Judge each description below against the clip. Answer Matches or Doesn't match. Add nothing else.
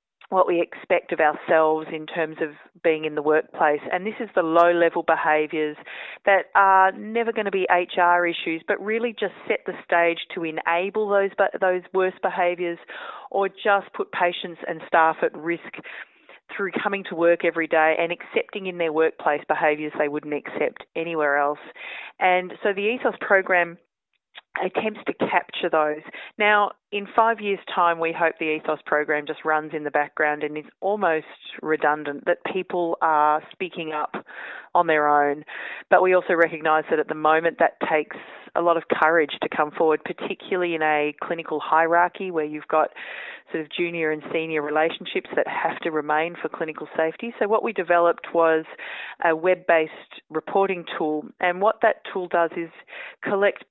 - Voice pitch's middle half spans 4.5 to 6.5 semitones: Doesn't match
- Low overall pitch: Doesn't match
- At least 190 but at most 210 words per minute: Doesn't match